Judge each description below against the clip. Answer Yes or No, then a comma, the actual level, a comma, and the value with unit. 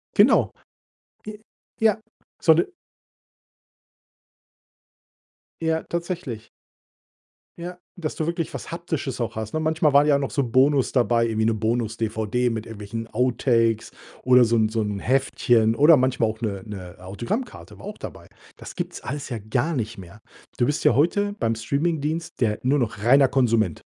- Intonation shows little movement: No, average, 5.2 semitones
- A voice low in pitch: Yes, low, 125 Hz